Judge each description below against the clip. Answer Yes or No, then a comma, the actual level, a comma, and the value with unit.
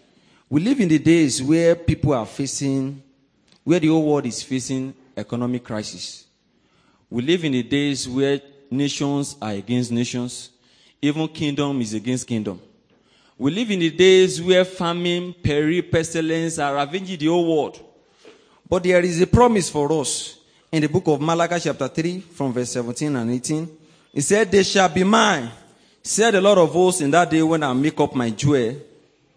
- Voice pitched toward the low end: No, medium, 150 Hz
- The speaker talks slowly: No, average, 175 wpm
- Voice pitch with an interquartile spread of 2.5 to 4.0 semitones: No, average, 4.7 semitones